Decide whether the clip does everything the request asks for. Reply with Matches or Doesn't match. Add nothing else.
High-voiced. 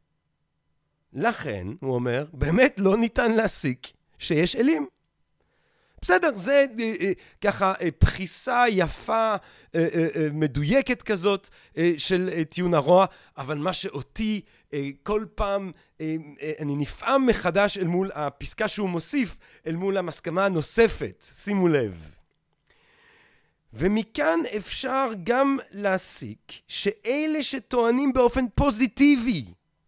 Matches